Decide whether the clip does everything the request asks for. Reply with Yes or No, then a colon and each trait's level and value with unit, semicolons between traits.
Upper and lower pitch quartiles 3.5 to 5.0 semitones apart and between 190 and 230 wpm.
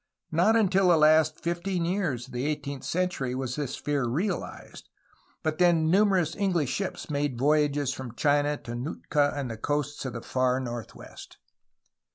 No: average, 4.6 semitones; average, 165 wpm